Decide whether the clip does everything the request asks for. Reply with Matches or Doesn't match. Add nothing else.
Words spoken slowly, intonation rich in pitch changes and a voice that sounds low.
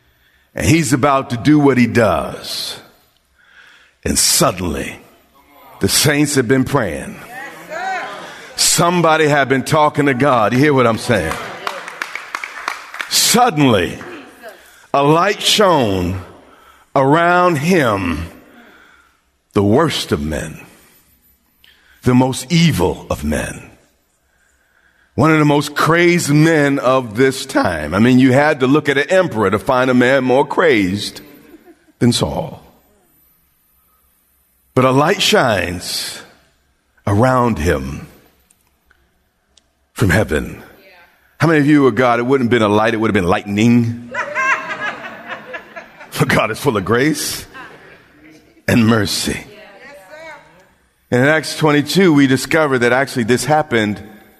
Matches